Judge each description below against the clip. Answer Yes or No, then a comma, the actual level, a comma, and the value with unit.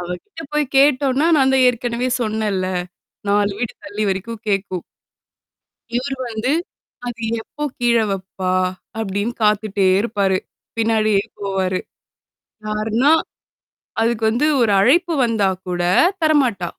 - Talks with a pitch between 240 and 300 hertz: No, high, 220 Hz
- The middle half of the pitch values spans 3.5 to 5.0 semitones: Yes, average, 3.8 semitones